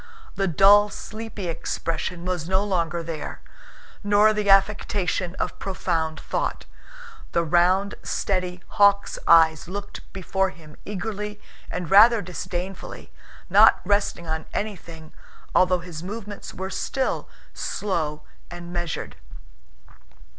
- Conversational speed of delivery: No, slow, 110 wpm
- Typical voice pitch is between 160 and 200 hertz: Yes, medium, 185 Hz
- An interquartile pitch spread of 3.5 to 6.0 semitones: No, average, 3.1 semitones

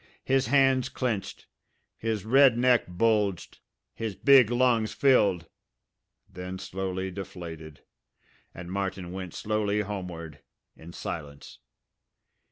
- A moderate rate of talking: No, slow, 100 wpm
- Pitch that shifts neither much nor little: Yes, average, 4.6 semitones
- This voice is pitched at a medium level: No, low, 100 Hz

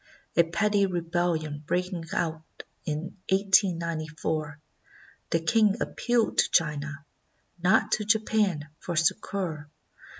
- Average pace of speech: No, slow, 105 wpm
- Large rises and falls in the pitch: No, average, 4.0 semitones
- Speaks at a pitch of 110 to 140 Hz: No, medium, 170 Hz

